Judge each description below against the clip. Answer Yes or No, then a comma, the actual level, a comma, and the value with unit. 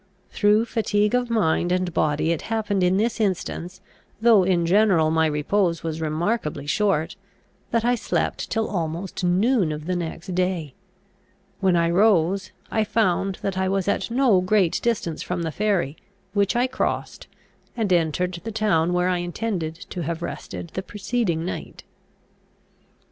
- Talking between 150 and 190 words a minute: Yes, average, 155 wpm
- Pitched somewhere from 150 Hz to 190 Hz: Yes, medium, 185 Hz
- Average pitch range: Yes, average, 4.0 semitones